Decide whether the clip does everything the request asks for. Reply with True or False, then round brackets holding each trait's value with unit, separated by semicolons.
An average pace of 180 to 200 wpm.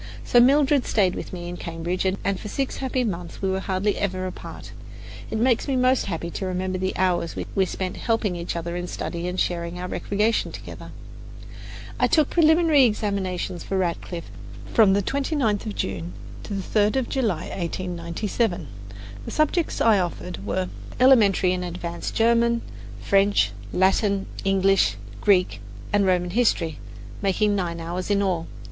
False (165 wpm)